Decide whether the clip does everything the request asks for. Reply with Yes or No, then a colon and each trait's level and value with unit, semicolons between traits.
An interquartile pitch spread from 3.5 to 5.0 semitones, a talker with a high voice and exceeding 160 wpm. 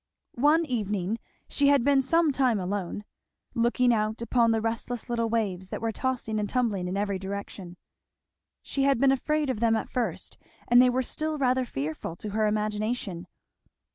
Yes: average, 3.9 semitones; high, 230 Hz; average, 170 wpm